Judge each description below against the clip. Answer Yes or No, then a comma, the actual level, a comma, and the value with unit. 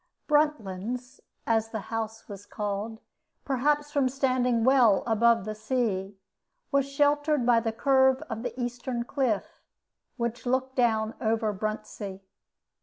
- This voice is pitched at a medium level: No, high, 235 Hz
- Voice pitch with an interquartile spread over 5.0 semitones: No, average, 3.3 semitones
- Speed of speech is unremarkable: No, slow, 125 wpm